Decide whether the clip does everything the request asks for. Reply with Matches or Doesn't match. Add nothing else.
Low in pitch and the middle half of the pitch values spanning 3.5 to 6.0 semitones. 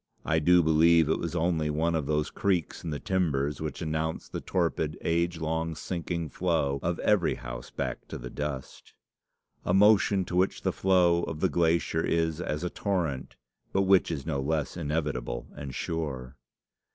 Doesn't match